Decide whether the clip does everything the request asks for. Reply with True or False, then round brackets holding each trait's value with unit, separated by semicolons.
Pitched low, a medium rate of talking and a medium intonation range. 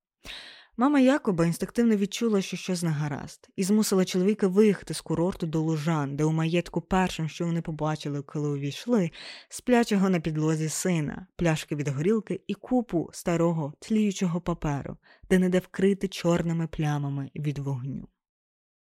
False (175 Hz; 145 wpm; 3.9 semitones)